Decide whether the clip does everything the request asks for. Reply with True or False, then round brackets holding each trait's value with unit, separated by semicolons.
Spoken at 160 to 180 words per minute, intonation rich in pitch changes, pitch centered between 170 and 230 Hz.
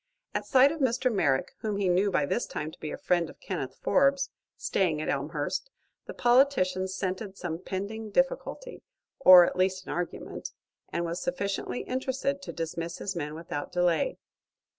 True (170 wpm; 6.9 semitones; 185 Hz)